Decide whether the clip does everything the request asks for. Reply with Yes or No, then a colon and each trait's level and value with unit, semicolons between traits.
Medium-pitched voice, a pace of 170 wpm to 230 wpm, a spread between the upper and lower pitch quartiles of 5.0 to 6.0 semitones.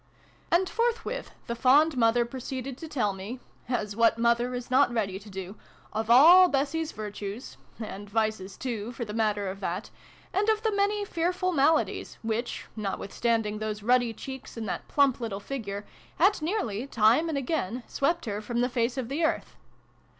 No: high, 240 Hz; average, 175 wpm; average, 5.3 semitones